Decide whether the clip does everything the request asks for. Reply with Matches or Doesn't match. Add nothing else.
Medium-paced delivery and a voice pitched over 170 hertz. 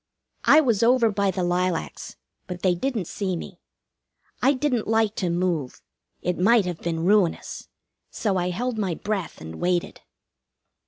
Matches